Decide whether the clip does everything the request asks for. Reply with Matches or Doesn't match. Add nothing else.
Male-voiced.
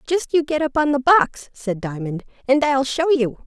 Doesn't match